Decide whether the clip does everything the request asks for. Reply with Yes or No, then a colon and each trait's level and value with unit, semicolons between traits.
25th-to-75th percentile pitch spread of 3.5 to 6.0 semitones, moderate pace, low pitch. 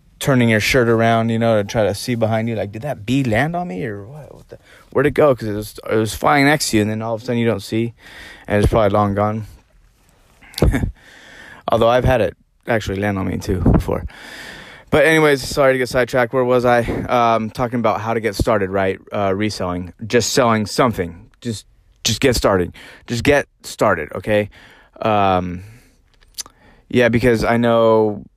No: average, 2.9 semitones; average, 195 wpm; low, 115 Hz